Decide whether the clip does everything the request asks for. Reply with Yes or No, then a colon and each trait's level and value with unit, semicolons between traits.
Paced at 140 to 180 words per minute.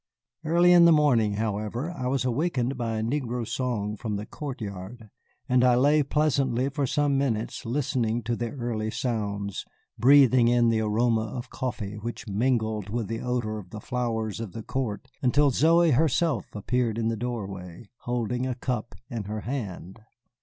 Yes: average, 170 wpm